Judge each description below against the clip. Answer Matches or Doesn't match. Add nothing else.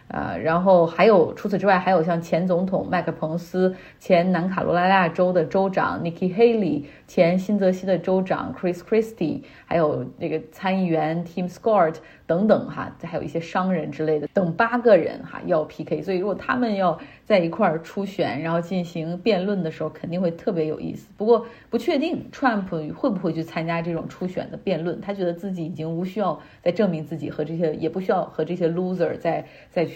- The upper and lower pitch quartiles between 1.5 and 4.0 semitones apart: Matches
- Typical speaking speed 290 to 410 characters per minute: Matches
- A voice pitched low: Doesn't match